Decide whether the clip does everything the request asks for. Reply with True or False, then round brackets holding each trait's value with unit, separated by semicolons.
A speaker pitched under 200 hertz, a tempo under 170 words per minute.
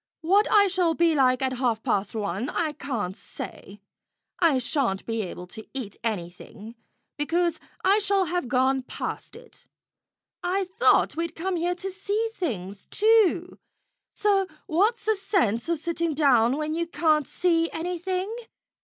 False (325 Hz; 150 wpm)